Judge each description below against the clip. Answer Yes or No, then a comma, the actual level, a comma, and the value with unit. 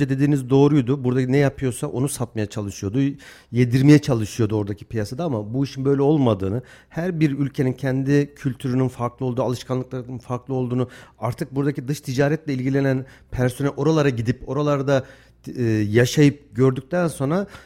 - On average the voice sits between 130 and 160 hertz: Yes, low, 135 Hz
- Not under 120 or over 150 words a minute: Yes, average, 135 wpm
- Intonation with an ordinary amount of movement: No, narrow, 2.2 semitones